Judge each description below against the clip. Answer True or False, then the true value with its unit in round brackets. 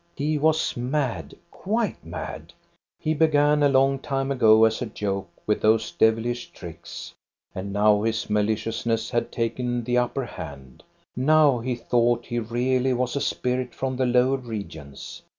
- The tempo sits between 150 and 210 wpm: True (155 wpm)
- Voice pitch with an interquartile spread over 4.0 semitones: False (3.4 semitones)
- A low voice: True (120 Hz)